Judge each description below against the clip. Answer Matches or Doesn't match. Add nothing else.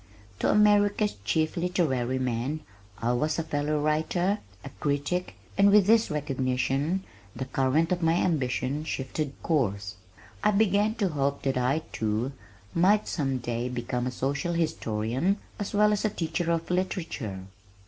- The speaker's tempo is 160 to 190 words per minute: Doesn't match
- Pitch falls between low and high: Matches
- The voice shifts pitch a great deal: Matches